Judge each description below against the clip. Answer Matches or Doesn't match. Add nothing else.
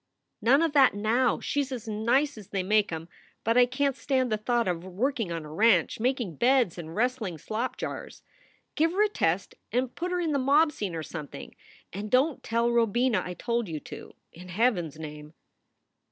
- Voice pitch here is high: Matches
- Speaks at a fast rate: Matches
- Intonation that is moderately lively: Doesn't match